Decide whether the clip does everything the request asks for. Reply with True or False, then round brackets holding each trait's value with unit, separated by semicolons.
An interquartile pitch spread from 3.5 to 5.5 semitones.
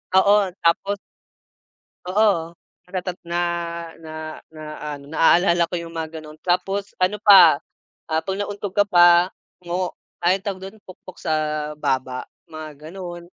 False (3.1 semitones)